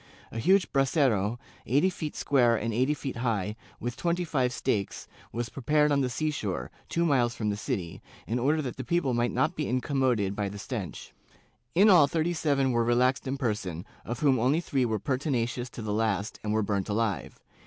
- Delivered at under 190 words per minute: No, average, 195 wpm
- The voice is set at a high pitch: No, low, 125 Hz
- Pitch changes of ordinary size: Yes, average, 4.7 semitones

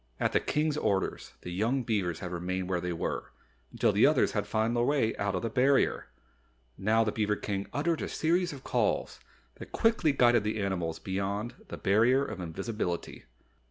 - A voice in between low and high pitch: No, low, 110 Hz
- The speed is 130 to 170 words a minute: No, average, 185 wpm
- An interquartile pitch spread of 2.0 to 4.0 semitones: No, average, 5.3 semitones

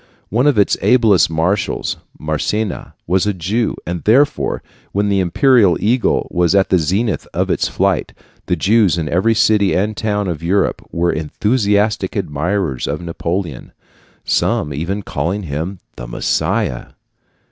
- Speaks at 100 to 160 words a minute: Yes, average, 145 wpm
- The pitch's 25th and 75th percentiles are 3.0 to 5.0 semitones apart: Yes, average, 3.9 semitones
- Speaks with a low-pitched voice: Yes, very low, 95 Hz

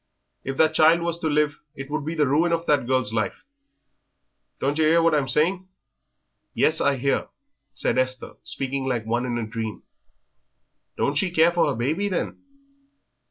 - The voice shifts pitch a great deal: No, average, 4.1 semitones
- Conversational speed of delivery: Yes, average, 175 wpm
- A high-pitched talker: No, medium, 145 Hz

